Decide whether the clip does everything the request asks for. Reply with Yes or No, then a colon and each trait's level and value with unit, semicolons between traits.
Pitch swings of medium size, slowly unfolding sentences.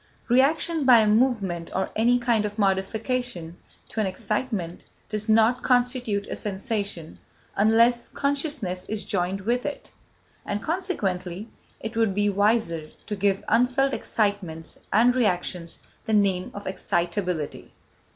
Yes: average, 4.4 semitones; slow, 130 wpm